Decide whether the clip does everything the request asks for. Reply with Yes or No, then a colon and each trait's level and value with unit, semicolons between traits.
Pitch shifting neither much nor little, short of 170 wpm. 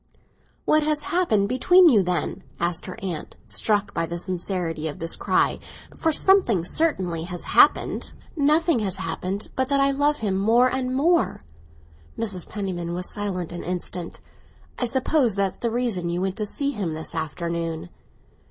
No: wide, 7.3 semitones; average, 160 wpm